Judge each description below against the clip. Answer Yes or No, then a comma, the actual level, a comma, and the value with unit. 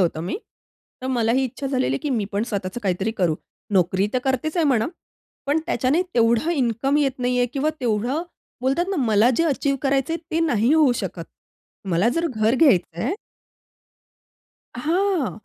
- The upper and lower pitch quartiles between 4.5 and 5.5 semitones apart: Yes, average, 5.0 semitones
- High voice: Yes, very high, 255 Hz